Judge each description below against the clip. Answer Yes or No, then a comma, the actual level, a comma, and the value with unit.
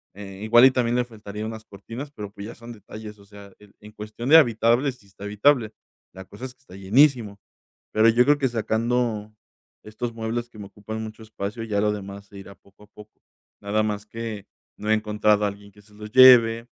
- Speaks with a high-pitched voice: No, low, 110 Hz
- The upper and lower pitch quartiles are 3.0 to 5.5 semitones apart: No, narrow, 2.4 semitones